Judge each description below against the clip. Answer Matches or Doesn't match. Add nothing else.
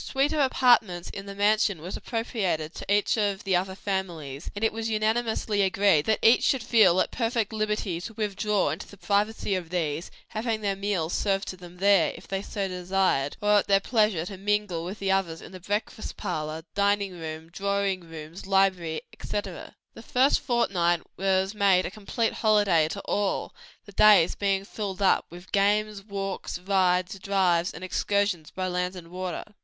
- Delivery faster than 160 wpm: Matches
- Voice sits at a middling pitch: Doesn't match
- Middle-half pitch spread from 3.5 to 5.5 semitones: Doesn't match